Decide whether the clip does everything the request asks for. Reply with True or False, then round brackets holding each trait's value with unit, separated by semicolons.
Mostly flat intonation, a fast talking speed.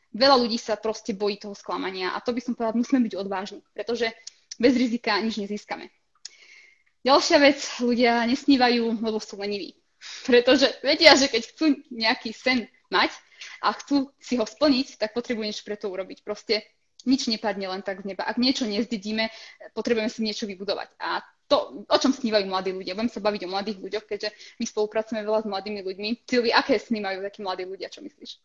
False (3.0 semitones; 185 wpm)